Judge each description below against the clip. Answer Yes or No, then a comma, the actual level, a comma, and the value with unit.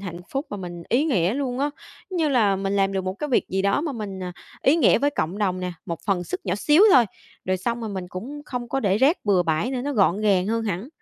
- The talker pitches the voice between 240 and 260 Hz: No, high, 205 Hz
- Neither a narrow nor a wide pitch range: No, wide, 6.0 semitones